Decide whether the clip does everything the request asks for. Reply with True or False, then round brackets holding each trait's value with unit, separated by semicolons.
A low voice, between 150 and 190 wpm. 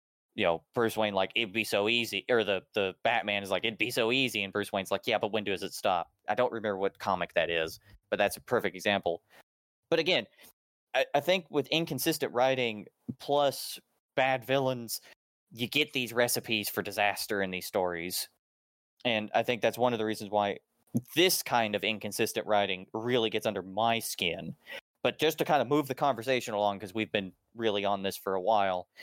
False (110 Hz; 205 wpm)